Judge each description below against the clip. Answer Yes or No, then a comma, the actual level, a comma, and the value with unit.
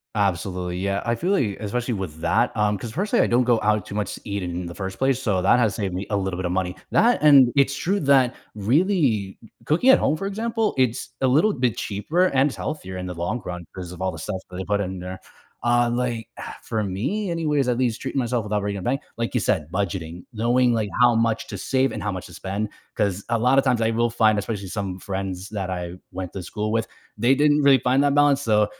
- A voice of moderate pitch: No, low, 110 Hz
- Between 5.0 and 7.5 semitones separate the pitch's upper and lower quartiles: Yes, wide, 5.5 semitones